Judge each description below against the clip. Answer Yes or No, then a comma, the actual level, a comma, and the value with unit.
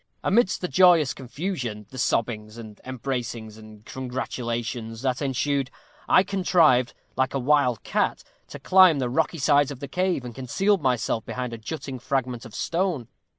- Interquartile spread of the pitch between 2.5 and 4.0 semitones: No, average, 4.7 semitones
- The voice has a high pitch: No, low, 130 Hz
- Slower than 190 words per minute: Yes, average, 155 wpm